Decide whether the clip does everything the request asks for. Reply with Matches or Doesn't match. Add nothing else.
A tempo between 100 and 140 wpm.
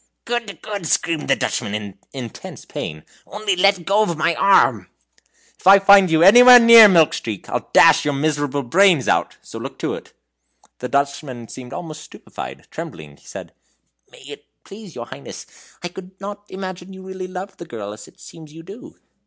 Doesn't match